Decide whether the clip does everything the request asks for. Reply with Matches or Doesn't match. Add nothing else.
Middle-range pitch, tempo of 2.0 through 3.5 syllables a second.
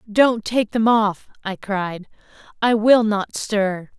Doesn't match